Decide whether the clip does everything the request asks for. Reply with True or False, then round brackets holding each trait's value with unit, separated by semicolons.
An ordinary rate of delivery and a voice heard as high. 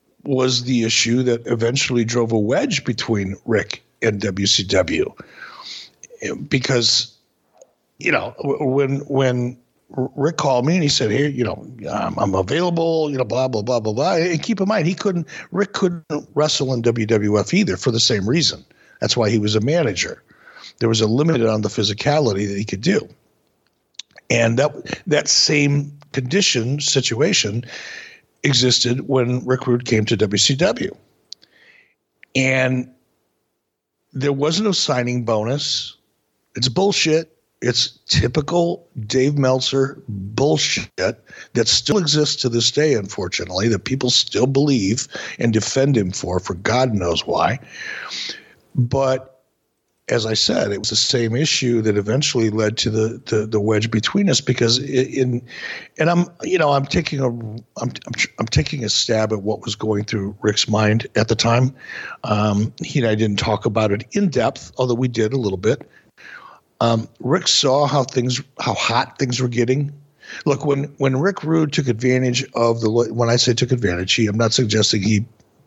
False (160 wpm; 125 Hz)